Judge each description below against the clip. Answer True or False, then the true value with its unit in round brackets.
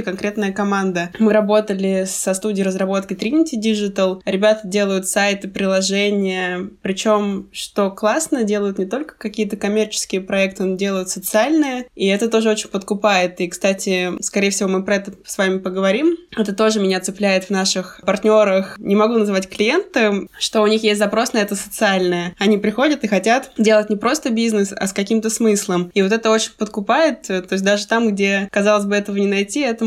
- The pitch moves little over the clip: True (2.1 semitones)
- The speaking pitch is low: False (205 Hz)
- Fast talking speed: True (175 wpm)